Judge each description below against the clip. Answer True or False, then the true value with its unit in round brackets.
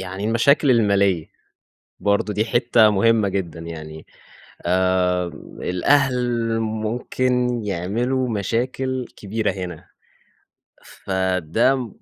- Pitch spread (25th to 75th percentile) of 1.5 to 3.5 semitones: False (4.7 semitones)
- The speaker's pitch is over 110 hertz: False (105 Hz)